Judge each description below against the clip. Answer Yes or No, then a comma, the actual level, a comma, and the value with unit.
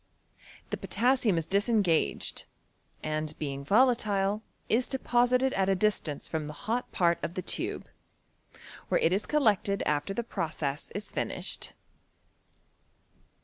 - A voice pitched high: Yes, high, 195 Hz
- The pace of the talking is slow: Yes, slow, 130 wpm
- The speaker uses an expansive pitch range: Yes, wide, 6.7 semitones